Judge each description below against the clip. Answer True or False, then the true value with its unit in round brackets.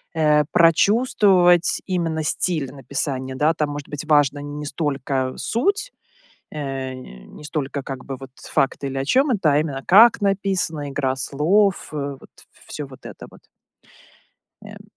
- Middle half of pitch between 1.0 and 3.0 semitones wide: False (4.5 semitones)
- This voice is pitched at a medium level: True (150 Hz)